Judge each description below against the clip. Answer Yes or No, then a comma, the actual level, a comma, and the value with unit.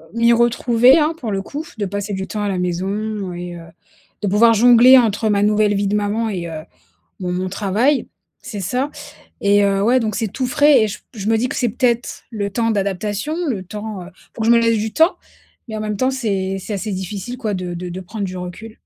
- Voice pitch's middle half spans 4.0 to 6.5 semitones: No, average, 3.2 semitones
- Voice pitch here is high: Yes, high, 210 Hz